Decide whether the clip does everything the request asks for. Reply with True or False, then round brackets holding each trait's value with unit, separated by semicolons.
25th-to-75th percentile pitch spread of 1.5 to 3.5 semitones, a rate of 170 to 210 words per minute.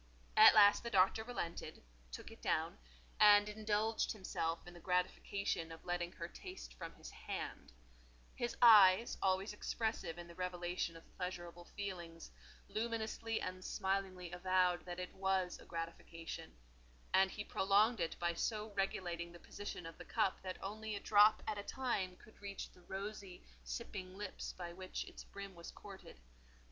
False (3.0 semitones; 160 wpm)